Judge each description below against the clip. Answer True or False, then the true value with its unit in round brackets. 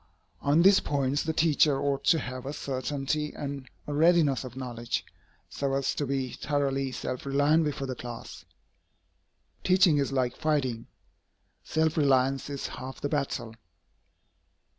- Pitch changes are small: True (2.3 semitones)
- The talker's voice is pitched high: False (140 Hz)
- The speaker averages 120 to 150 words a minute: True (140 wpm)